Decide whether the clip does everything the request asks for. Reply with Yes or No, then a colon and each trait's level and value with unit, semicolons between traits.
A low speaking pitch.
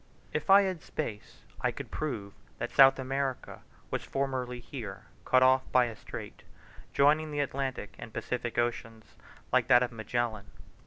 Yes: low, 130 Hz